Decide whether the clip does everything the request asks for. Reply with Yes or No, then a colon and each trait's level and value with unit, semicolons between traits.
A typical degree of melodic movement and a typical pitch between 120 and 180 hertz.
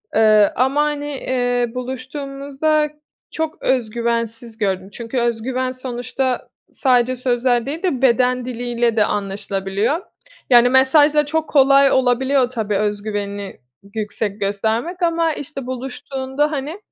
No: average, 3.3 semitones; very high, 250 Hz